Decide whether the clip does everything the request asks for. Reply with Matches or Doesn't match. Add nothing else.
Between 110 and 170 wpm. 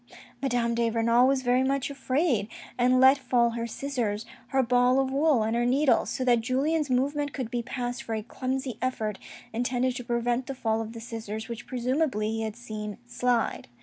Doesn't match